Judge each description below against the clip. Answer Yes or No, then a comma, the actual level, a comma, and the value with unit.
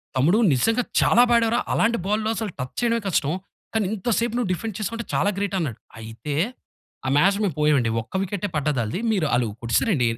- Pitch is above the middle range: Yes, high, 195 Hz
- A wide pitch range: Yes, wide, 8.2 semitones